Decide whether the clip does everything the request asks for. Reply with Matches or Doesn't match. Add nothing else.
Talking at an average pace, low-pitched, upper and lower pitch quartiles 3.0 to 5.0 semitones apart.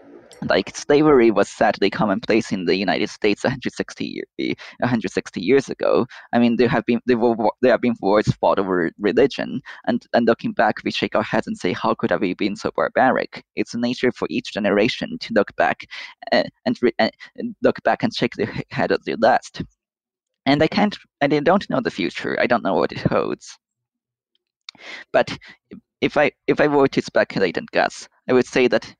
Matches